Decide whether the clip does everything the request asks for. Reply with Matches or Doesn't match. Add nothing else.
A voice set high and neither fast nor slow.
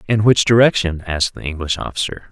Doesn't match